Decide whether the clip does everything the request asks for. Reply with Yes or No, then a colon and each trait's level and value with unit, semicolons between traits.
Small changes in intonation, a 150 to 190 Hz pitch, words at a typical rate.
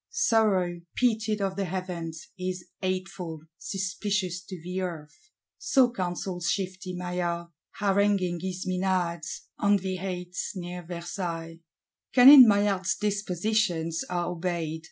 No: narrow, 2.3 semitones; medium, 185 Hz; slow, 110 wpm